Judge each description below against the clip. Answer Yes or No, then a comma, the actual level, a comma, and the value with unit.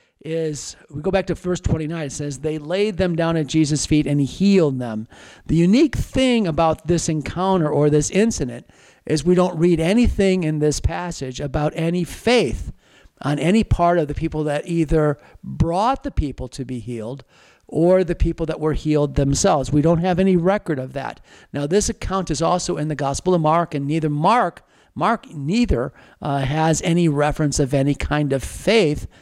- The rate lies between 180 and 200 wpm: Yes, average, 185 wpm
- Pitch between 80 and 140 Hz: No, medium, 160 Hz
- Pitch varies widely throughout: No, average, 3.5 semitones